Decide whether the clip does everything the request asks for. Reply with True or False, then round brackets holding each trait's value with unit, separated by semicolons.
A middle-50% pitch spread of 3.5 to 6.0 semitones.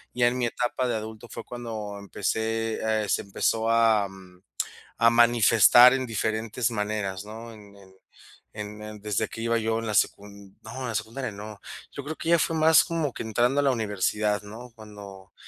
False (2.5 semitones)